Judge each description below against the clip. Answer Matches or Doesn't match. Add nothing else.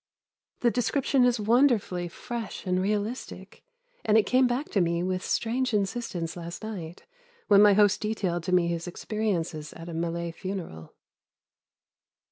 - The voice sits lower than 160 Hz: Doesn't match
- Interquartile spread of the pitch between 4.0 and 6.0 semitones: Matches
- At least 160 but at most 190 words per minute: Doesn't match